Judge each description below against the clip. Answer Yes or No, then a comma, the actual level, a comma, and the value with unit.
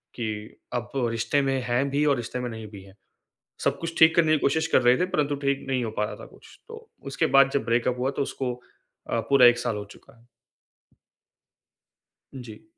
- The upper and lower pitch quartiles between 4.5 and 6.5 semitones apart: No, average, 3.2 semitones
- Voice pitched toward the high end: No, low, 125 Hz